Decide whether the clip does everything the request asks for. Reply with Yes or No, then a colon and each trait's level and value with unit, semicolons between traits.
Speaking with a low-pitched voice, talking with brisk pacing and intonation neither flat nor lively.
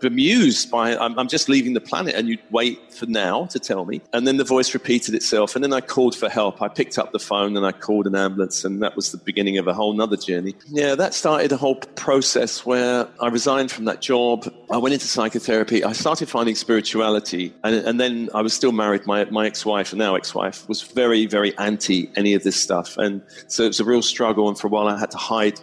Yes: low, 110 Hz; fast, 250 wpm; average, 3.1 semitones